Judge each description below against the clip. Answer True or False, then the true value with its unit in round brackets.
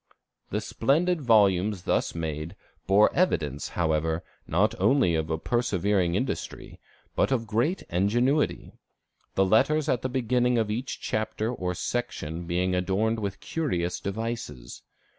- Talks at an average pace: False (125 wpm)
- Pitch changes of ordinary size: False (5.8 semitones)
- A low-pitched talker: True (105 Hz)